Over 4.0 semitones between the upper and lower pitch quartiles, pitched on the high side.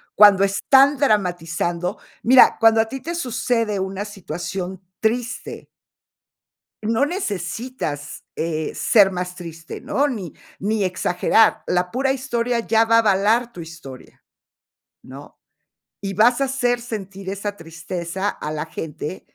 Yes: average, 5.0 semitones; high, 205 Hz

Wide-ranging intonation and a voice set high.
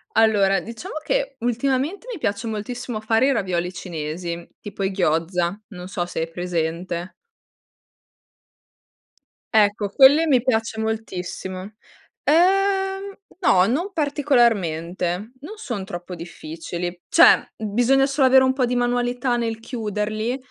Yes: wide, 6.4 semitones; high, 220 Hz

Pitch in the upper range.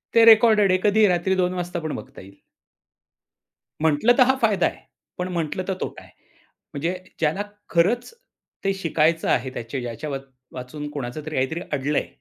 No: medium, 165 Hz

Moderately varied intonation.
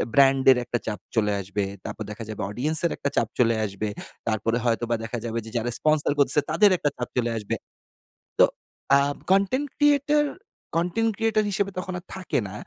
No: wide, 8.9 semitones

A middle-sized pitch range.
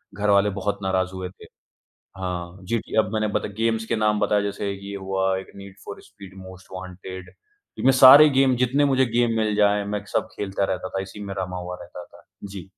No: narrow, 2.2 semitones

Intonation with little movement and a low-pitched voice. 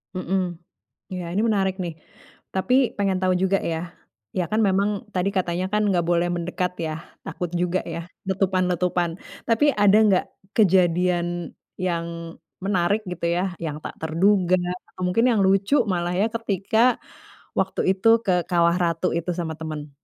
No: narrow, 2.1 semitones; medium, 185 Hz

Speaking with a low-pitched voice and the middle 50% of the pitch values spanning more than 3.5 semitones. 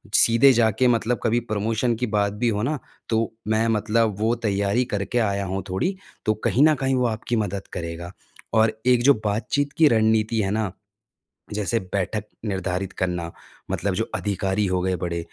No: low, 110 Hz; average, 3.0 semitones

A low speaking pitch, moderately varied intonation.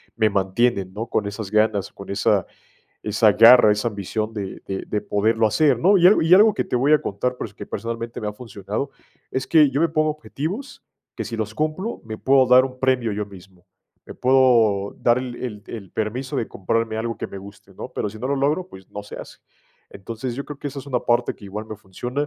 Yes: low, 115 Hz; average, 4.2 semitones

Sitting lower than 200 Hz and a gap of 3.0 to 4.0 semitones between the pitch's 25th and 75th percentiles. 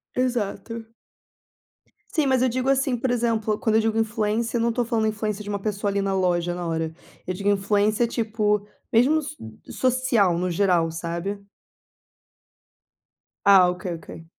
No: high, 210 Hz; average, 3.3 semitones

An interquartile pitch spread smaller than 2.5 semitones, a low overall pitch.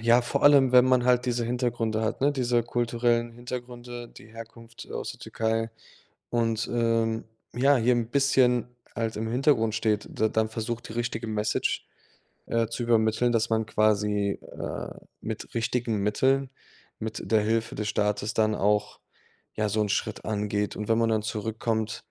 Yes: narrow, 1.8 semitones; low, 115 Hz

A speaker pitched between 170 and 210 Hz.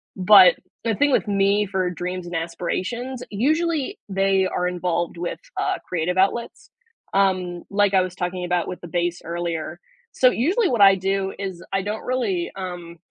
Yes: high, 190 Hz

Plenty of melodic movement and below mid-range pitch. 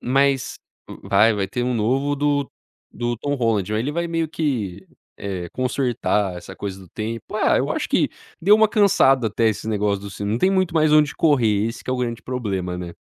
Yes: wide, 5.8 semitones; low, 120 Hz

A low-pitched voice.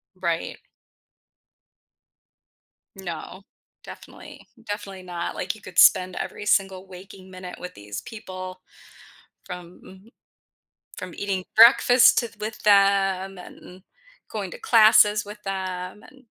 No: high, 190 Hz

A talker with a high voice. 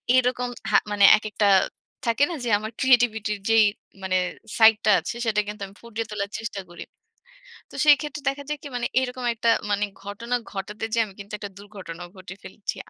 Yes: high, 220 Hz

